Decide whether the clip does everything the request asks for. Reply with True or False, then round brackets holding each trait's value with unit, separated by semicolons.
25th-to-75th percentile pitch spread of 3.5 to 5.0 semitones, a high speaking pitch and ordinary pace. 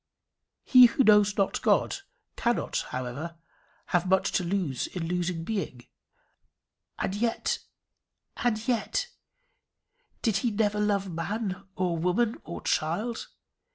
False (4.2 semitones; 195 Hz; 120 wpm)